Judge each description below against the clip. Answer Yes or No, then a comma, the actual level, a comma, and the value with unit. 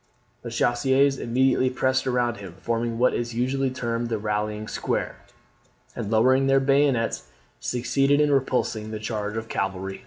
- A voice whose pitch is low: Yes, low, 120 Hz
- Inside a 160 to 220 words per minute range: No, average, 150 wpm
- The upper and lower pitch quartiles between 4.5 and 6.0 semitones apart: No, average, 3.2 semitones